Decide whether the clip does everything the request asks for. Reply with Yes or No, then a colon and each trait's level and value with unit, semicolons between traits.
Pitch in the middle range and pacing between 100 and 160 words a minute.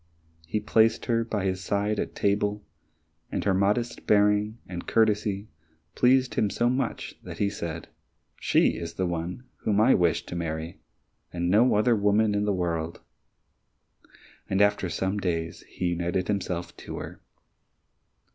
No: low, 100 Hz; average, 150 wpm